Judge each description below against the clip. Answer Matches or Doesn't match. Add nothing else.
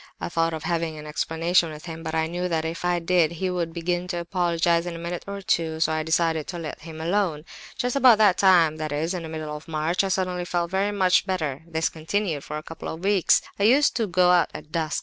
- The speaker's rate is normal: Doesn't match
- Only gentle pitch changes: Matches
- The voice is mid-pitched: Matches